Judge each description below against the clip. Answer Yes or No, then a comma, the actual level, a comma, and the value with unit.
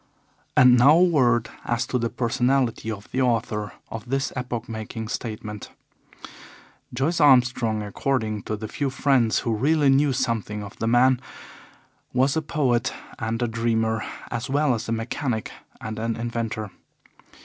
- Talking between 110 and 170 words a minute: Yes, average, 150 wpm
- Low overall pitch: Yes, low, 120 Hz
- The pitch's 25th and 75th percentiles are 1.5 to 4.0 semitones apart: Yes, average, 3.0 semitones